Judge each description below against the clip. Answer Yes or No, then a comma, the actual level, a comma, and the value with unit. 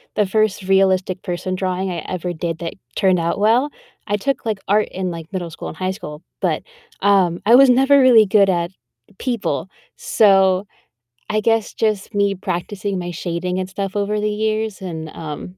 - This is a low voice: No, high, 190 Hz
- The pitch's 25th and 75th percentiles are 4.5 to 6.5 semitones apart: No, average, 3.0 semitones